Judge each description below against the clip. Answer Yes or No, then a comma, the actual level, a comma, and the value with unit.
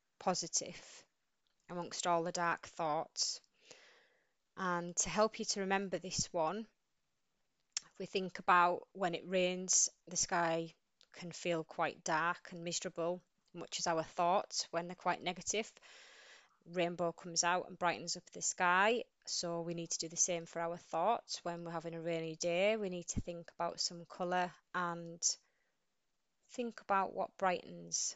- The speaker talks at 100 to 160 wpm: Yes, average, 155 wpm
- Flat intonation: Yes, narrow, 1.7 semitones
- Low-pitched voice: No, medium, 175 Hz